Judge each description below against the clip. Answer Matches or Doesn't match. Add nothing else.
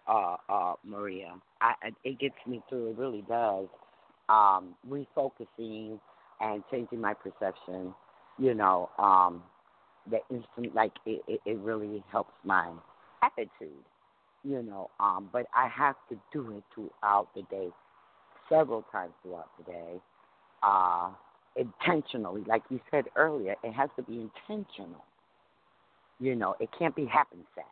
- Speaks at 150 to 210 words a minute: Doesn't match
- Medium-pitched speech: Doesn't match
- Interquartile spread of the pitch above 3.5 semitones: Matches